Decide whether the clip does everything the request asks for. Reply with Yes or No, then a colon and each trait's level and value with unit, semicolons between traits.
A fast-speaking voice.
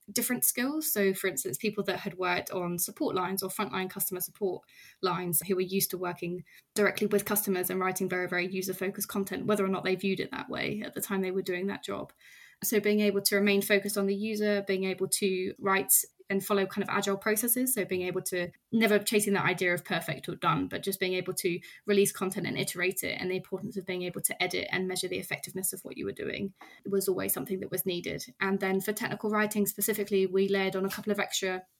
Yes: fast, 240 wpm